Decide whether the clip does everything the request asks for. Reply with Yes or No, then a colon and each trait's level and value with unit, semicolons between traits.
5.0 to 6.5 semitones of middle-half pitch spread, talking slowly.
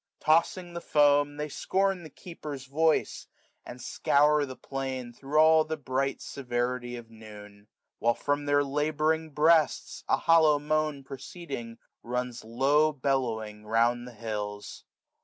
No: average, 4.2 semitones; slow, 130 wpm